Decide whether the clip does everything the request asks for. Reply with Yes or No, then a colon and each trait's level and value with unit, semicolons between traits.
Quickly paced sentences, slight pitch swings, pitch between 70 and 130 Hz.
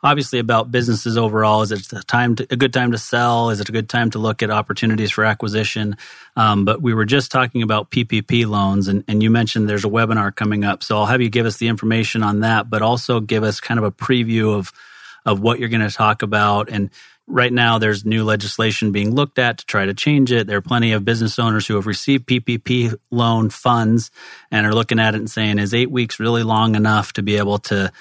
Yes: fast, 240 wpm; narrow, 2.0 semitones; low, 110 Hz